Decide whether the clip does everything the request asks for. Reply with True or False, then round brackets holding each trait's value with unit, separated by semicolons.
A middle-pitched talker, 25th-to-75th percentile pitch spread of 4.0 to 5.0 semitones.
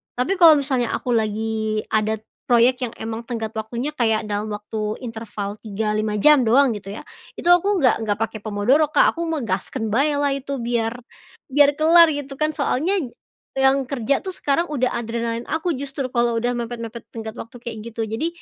False (235 Hz; 4.3 semitones)